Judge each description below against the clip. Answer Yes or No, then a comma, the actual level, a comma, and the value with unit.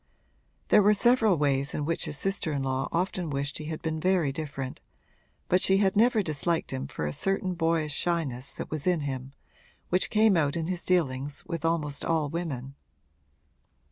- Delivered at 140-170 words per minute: No, average, 180 wpm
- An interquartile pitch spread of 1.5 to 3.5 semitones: No, average, 4.4 semitones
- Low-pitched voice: No, medium, 160 Hz